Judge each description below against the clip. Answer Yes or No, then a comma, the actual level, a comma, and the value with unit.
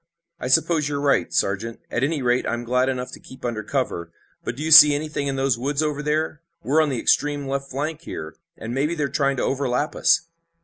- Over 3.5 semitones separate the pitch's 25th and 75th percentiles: No, average, 3.0 semitones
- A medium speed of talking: No, fast, 220 wpm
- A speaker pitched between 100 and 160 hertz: Yes, medium, 140 Hz